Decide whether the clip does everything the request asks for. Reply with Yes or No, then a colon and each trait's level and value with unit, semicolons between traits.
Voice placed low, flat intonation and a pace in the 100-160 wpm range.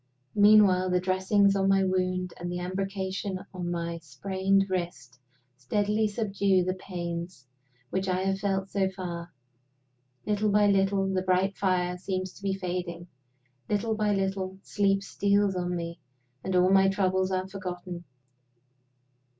No: high, 190 Hz; narrow, 1.4 semitones; average, 140 wpm